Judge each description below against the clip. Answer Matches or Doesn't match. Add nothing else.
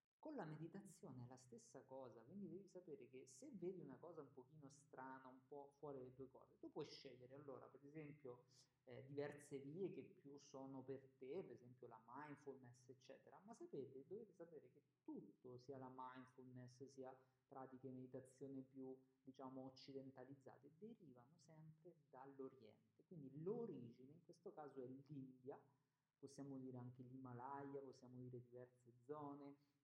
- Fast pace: Doesn't match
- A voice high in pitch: Doesn't match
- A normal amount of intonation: Doesn't match